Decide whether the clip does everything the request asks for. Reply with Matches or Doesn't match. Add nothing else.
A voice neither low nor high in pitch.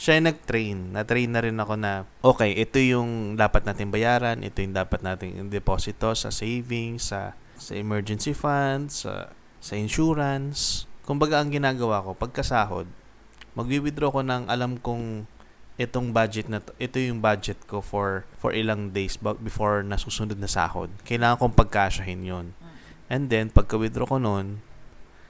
Doesn't match